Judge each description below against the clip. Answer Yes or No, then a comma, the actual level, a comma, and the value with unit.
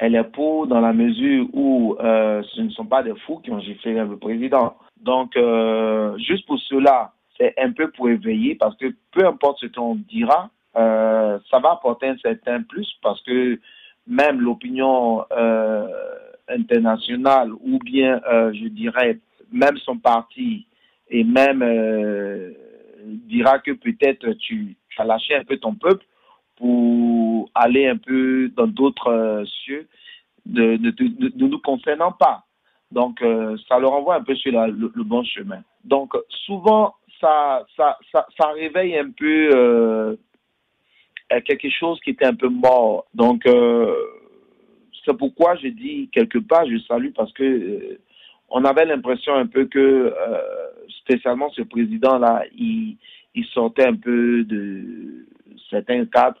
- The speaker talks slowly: No, average, 155 wpm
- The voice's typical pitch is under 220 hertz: Yes, low, 135 Hz